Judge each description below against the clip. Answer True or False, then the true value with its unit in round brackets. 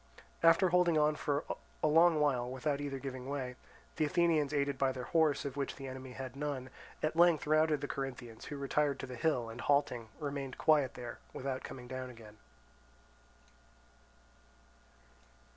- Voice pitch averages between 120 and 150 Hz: True (140 Hz)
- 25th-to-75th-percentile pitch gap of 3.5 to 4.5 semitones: False (2.8 semitones)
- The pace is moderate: True (160 wpm)